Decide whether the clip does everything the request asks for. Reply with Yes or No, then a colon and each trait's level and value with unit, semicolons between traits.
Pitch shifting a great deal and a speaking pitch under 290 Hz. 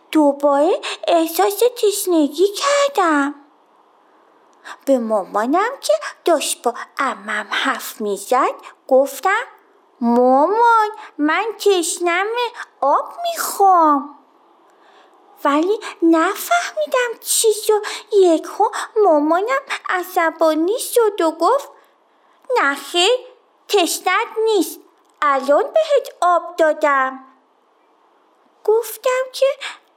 No: wide, 5.8 semitones; very high, 350 Hz